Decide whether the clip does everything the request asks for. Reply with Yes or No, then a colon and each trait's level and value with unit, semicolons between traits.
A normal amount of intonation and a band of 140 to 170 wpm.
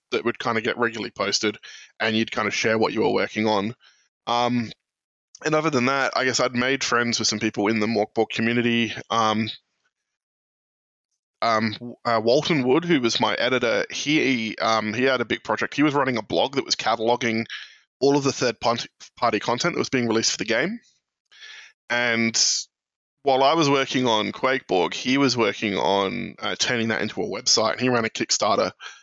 No: average, 3.1 semitones; average, 190 wpm